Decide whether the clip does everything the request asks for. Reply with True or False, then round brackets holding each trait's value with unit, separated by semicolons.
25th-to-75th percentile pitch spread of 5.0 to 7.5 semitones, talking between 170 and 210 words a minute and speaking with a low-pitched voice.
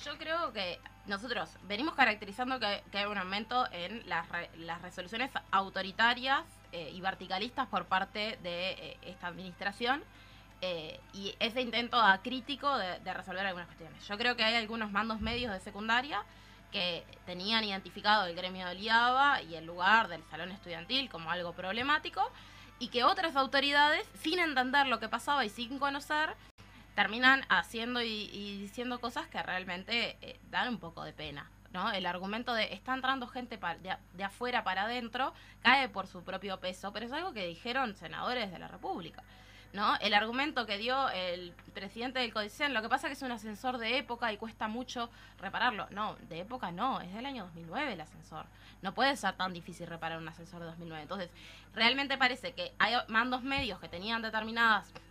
False (5.6 semitones; 180 wpm; 220 Hz)